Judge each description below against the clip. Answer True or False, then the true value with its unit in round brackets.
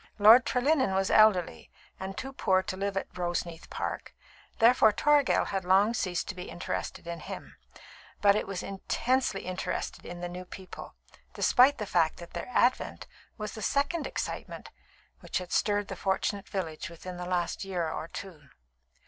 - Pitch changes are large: False (3.5 semitones)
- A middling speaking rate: True (165 wpm)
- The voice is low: False (195 Hz)